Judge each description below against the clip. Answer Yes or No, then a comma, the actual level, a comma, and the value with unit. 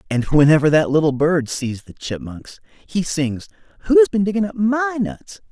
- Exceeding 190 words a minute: No, average, 165 wpm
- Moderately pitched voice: Yes, medium, 170 Hz